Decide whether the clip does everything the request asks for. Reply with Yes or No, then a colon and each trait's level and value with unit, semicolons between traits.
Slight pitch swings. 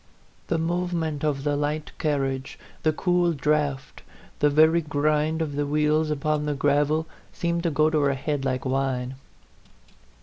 Yes: narrow, 1.9 semitones